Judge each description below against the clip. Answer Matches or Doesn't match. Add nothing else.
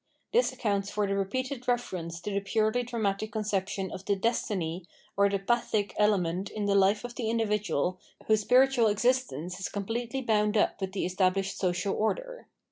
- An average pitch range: Matches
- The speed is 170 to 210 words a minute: Matches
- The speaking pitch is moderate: Doesn't match